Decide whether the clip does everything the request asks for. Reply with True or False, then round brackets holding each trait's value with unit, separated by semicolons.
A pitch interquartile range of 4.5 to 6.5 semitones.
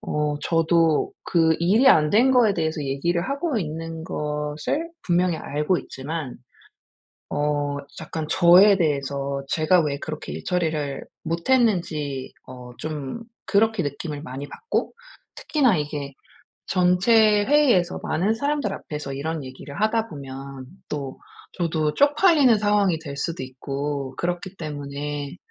True (5.4 semitones)